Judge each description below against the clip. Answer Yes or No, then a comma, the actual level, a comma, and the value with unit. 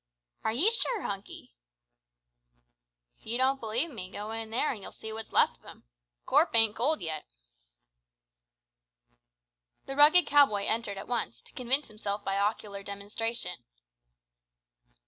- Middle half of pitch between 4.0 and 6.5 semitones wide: Yes, average, 4.5 semitones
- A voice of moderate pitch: No, high, 225 Hz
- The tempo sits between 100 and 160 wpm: Yes, average, 145 wpm